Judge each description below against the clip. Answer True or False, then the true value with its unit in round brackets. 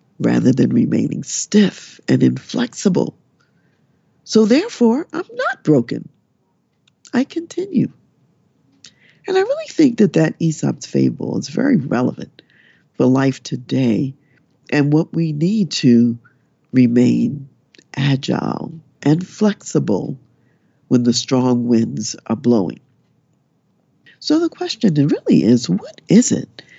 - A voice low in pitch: False (145 Hz)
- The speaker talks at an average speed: False (110 wpm)